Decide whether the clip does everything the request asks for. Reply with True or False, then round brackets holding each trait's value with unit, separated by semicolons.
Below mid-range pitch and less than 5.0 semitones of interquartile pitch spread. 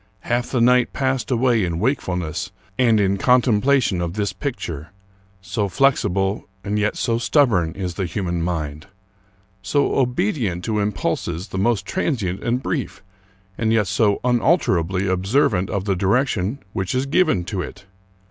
False (105 Hz; 5.4 semitones)